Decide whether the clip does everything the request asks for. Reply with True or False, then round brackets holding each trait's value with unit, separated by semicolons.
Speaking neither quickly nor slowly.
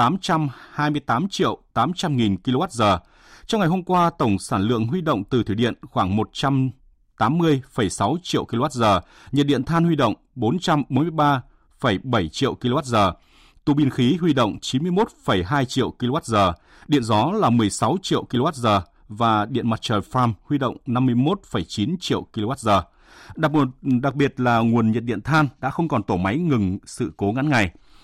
False (150 wpm)